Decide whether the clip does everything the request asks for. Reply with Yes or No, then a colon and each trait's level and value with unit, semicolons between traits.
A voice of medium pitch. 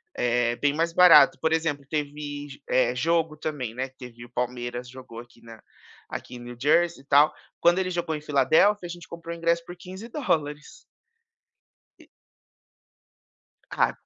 Yes: medium, 150 Hz